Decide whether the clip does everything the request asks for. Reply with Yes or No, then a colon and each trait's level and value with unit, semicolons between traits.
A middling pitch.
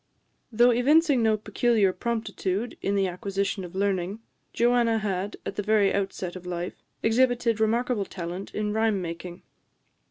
No: high, 210 Hz